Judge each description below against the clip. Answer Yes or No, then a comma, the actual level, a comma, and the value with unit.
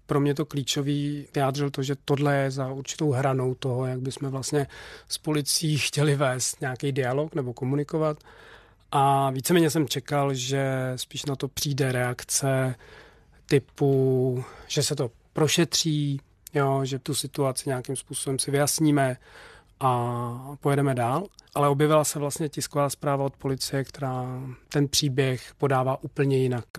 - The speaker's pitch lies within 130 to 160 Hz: Yes, medium, 140 Hz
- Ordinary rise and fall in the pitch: No, narrow, 1.9 semitones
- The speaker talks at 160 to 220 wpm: No, average, 145 wpm